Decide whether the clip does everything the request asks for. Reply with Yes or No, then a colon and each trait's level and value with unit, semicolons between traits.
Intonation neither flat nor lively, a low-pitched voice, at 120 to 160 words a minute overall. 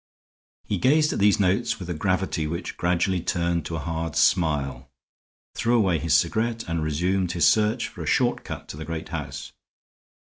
No: average, 3.6 semitones; very low, 85 Hz; average, 180 wpm